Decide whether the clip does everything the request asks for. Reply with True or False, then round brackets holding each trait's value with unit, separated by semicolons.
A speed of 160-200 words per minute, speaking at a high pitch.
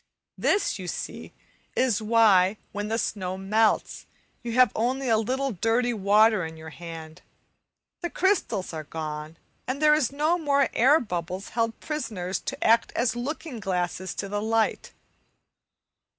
False (150 wpm; 220 Hz)